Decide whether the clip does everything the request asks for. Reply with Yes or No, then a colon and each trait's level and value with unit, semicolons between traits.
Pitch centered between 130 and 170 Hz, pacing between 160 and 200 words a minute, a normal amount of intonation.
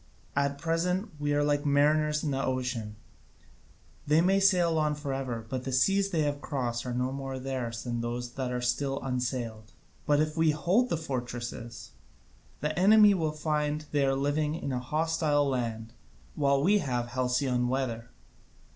Yes: medium, 140 Hz; average, 170 wpm; average, 3.6 semitones